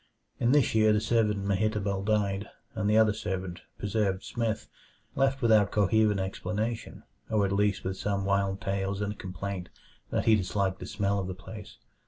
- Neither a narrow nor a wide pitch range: No, narrow, 1.8 semitones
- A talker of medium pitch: No, low, 100 Hz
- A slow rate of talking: No, average, 180 wpm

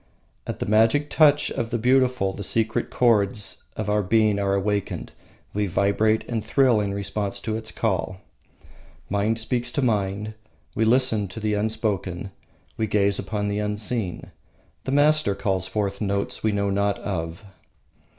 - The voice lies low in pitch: Yes, low, 105 Hz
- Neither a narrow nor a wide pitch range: No, narrow, 2.2 semitones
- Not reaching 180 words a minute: Yes, average, 155 wpm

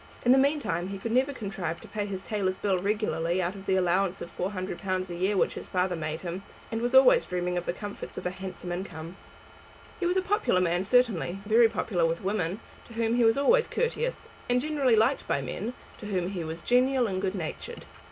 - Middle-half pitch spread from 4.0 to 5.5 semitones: Yes, average, 4.9 semitones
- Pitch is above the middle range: Yes, high, 195 Hz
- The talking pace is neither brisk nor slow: No, fast, 220 wpm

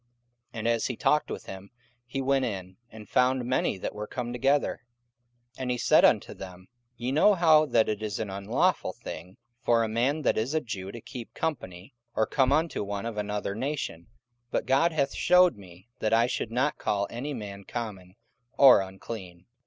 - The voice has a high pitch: No, low, 115 Hz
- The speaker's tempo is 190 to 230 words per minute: Yes, average, 195 wpm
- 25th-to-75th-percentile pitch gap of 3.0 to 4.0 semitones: No, average, 5.1 semitones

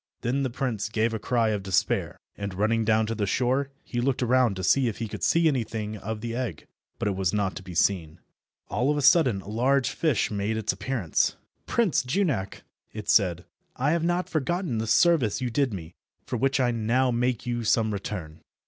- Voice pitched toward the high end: No, low, 115 Hz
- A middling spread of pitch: Yes, average, 4.1 semitones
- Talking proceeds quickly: Yes, fast, 210 wpm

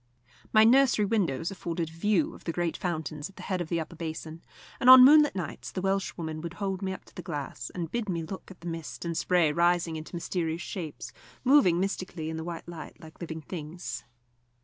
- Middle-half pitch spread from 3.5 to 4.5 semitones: No, average, 3.1 semitones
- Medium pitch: Yes, medium, 170 Hz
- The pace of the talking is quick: Yes, fast, 215 wpm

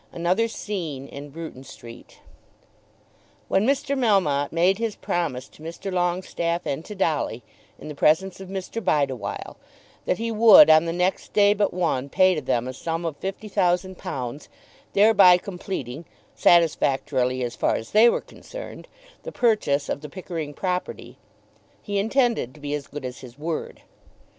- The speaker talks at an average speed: Yes, average, 160 wpm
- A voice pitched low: No, medium, 170 Hz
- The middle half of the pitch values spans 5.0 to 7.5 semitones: Yes, wide, 5.6 semitones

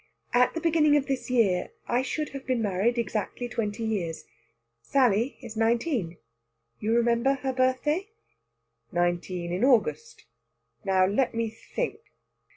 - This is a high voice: Yes, high, 235 Hz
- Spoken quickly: No, slow, 135 wpm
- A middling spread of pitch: Yes, average, 4.6 semitones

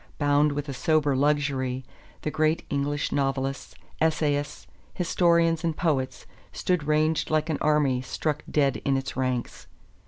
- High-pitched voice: No, medium, 145 Hz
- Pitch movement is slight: Yes, narrow, 2.3 semitones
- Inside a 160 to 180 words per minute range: No, slow, 135 wpm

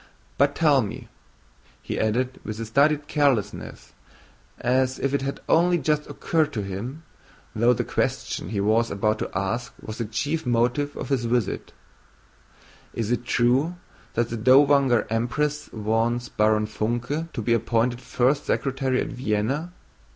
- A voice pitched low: Yes, low, 125 Hz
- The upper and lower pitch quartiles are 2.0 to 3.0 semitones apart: No, average, 3.9 semitones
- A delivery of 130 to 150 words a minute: Yes, average, 145 wpm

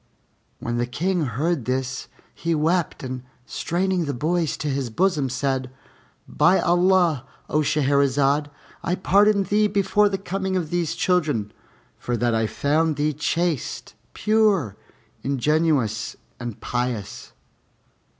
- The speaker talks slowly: Yes, slow, 125 wpm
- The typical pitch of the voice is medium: Yes, medium, 150 Hz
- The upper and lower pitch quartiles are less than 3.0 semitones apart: No, wide, 5.6 semitones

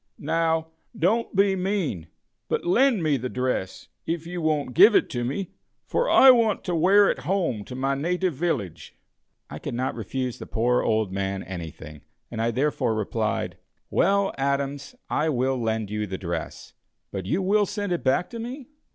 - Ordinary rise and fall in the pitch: No, wide, 8.6 semitones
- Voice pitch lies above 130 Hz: Yes, medium, 140 Hz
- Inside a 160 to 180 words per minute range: Yes, average, 175 wpm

